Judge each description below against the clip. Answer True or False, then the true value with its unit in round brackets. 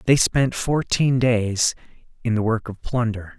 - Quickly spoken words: False (160 wpm)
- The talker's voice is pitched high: False (115 Hz)